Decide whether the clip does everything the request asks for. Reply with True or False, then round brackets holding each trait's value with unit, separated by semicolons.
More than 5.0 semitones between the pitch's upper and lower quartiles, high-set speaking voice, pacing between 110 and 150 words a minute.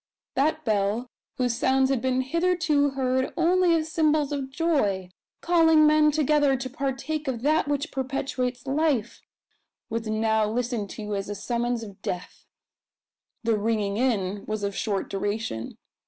True (5.6 semitones; 260 Hz; 145 wpm)